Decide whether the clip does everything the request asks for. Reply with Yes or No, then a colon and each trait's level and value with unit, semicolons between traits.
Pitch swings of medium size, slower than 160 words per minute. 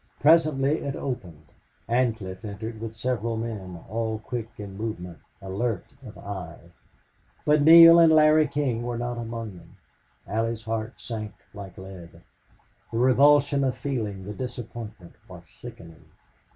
Yes: average, 4.4 semitones; slow, 135 wpm